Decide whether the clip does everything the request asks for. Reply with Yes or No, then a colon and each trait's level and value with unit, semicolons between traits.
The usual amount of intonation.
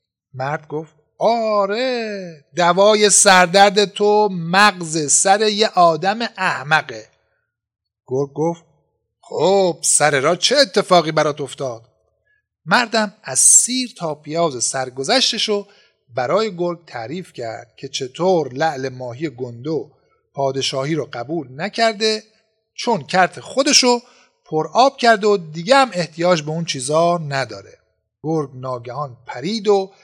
No: wide, 7.0 semitones